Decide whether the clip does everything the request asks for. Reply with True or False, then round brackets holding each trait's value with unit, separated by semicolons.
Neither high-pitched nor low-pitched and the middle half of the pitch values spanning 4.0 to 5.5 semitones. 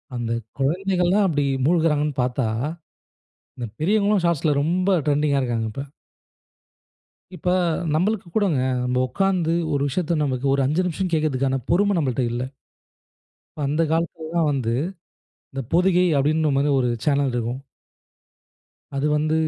True (150 Hz; 4.6 semitones)